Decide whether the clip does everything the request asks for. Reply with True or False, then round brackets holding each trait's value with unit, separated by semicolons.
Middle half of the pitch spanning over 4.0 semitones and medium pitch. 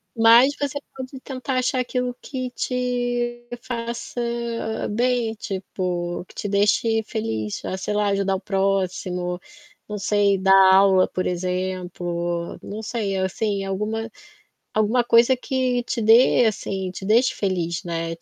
False (4.4 semitones; 210 Hz)